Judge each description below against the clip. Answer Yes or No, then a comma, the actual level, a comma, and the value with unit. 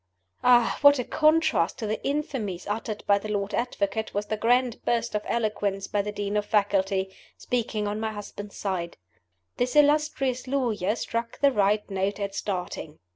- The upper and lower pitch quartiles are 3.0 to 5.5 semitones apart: Yes, average, 3.5 semitones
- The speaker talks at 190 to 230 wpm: No, average, 170 wpm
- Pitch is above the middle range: Yes, high, 210 Hz